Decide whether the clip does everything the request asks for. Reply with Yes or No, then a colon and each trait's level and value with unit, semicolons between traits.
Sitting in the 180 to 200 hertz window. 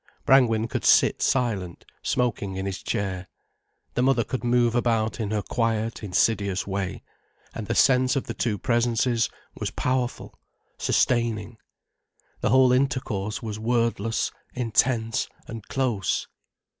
No: low, 115 Hz